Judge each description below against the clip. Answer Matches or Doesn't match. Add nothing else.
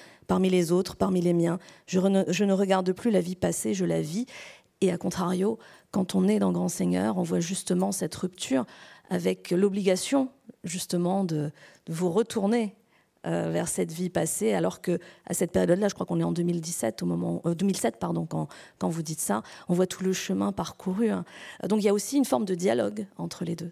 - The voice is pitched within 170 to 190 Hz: Matches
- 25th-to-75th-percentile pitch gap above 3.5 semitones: Doesn't match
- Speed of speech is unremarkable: Matches